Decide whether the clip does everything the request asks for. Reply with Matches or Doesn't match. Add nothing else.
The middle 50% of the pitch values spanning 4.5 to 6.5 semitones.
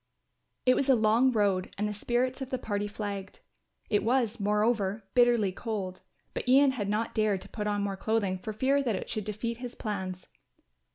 Doesn't match